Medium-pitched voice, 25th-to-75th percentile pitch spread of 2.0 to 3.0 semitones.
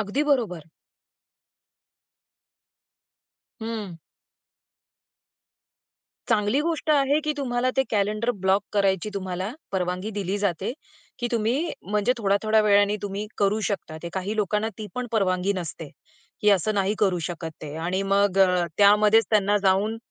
No: high, 205 Hz; narrow, 2.5 semitones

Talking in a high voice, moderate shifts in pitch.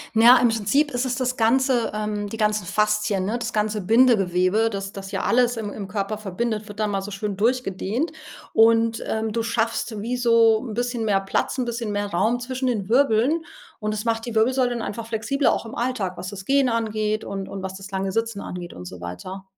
Yes: high, 220 Hz; average, 3.0 semitones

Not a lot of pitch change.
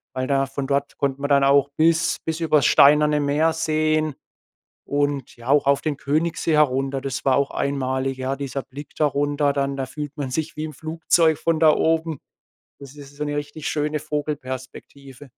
Yes: narrow, 2.0 semitones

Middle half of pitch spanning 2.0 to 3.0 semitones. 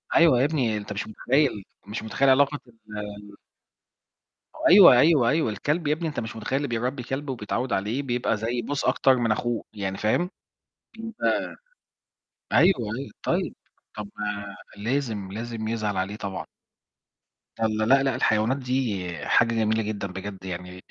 No: average, 4.5 semitones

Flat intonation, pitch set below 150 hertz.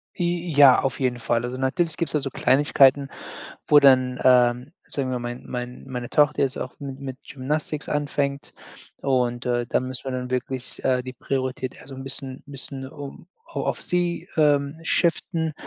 Yes: narrow, 2.3 semitones; low, 135 Hz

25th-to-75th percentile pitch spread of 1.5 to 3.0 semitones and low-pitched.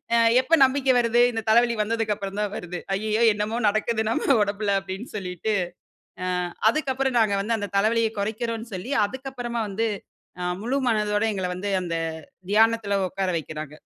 No: average, 2.7 semitones; high, 220 Hz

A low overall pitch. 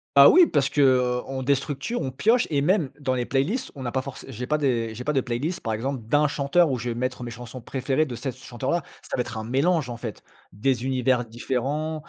Yes: low, 130 Hz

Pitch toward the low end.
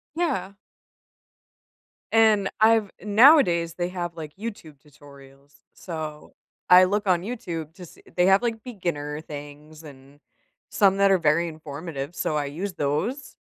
No: medium, 170 Hz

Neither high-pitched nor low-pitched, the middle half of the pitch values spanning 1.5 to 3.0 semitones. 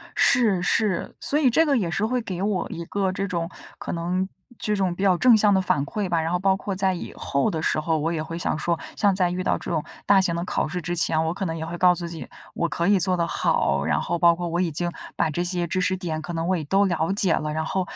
Yes: medium, 180 Hz; narrow, 2.5 semitones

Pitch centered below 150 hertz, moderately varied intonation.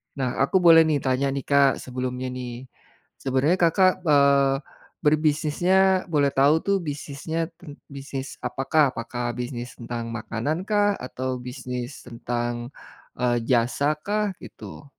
Yes: medium, 140 Hz; average, 4.0 semitones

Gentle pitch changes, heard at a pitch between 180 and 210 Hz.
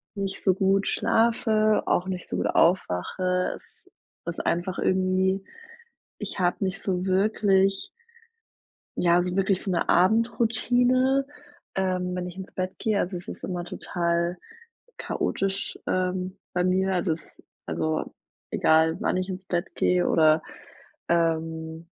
Yes: narrow, 1.9 semitones; medium, 185 Hz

